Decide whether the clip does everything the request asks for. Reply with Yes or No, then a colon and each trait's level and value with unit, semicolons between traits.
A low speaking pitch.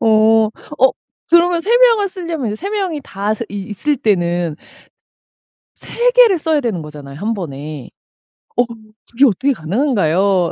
No: high, 225 Hz